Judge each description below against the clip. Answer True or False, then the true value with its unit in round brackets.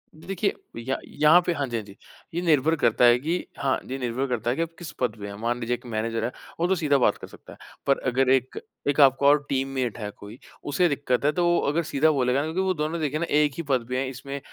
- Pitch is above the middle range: False (140 Hz)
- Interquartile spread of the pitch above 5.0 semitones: False (4.0 semitones)